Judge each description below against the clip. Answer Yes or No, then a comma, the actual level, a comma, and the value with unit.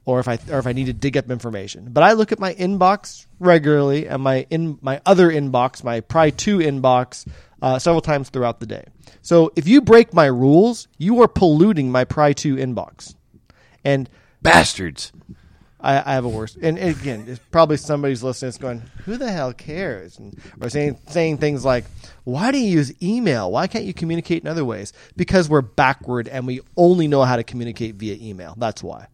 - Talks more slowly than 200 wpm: No, fast, 205 wpm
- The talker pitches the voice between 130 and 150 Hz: Yes, medium, 140 Hz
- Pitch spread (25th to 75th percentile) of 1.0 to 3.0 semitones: No, average, 5.1 semitones